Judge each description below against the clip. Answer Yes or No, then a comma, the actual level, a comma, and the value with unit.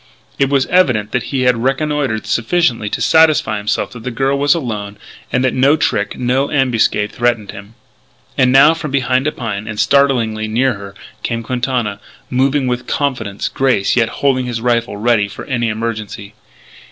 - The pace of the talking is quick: No, average, 170 wpm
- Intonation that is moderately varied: Yes, average, 3.8 semitones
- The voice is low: Yes, low, 125 Hz